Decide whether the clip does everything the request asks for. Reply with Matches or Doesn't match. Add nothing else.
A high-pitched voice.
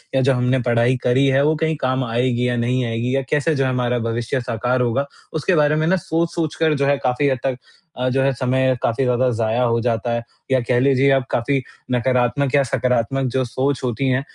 Doesn't match